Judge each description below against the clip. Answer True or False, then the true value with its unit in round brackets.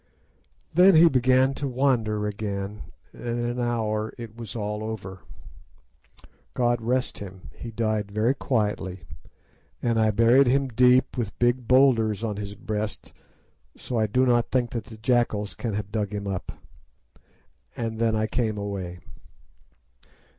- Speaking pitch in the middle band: False (110 Hz)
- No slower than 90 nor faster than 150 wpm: True (145 wpm)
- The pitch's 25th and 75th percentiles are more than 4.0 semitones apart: False (2.8 semitones)